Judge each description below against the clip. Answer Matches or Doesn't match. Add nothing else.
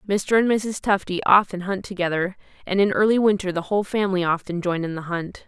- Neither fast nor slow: Doesn't match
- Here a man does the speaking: Doesn't match